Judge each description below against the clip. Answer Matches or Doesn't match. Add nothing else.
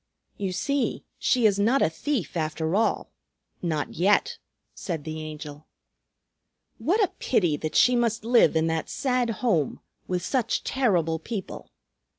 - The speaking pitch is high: Matches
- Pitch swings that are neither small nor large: Doesn't match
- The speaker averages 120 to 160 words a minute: Matches